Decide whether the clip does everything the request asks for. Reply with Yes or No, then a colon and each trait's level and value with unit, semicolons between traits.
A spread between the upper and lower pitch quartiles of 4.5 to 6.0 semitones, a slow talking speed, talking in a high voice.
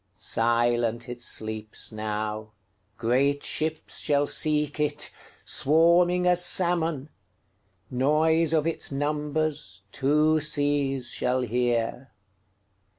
No: wide, 5.6 semitones; slow, 75 wpm; low, 135 Hz